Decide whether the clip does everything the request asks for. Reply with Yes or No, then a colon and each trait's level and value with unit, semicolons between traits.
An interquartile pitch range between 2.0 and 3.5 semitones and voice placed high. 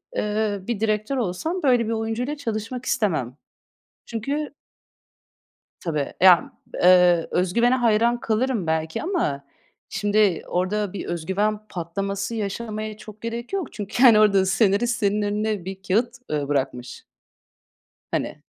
No: average, 4.1 semitones; high, 210 Hz